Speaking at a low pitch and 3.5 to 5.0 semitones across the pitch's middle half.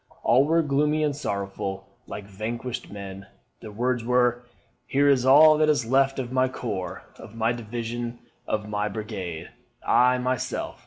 Yes: low, 120 Hz; average, 3.9 semitones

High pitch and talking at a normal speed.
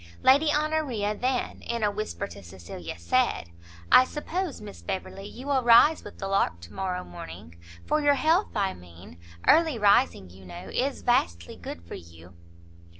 Yes: high, 205 Hz; average, 165 wpm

